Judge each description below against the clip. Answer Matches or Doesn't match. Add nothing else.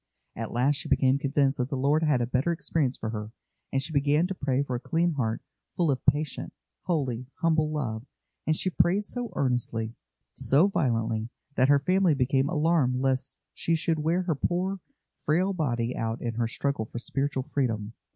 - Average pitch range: Matches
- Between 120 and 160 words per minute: Doesn't match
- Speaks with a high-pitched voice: Doesn't match